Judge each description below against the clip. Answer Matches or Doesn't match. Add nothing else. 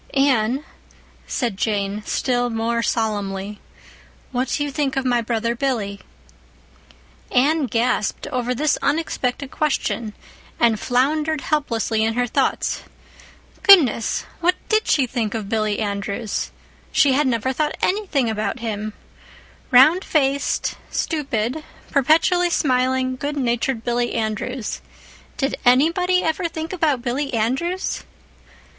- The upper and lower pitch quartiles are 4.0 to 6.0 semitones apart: Matches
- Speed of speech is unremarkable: Doesn't match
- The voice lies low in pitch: Doesn't match